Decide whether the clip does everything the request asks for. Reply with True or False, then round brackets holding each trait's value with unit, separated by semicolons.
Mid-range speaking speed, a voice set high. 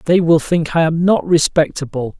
False (190 wpm; 160 Hz)